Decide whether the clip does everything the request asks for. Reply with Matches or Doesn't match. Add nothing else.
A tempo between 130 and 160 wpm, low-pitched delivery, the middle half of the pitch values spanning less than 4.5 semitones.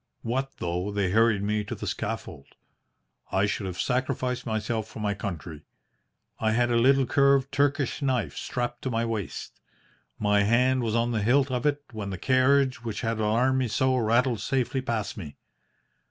Doesn't match